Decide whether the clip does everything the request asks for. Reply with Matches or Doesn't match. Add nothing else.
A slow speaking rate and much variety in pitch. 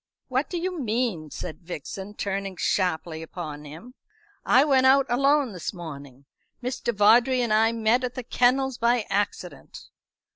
Doesn't match